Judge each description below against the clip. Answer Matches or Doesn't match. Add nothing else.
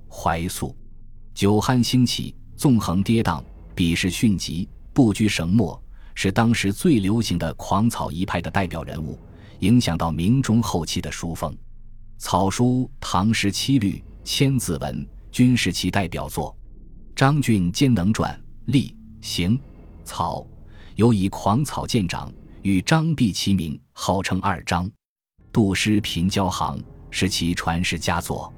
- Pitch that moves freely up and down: Doesn't match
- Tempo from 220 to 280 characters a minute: Doesn't match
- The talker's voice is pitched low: Matches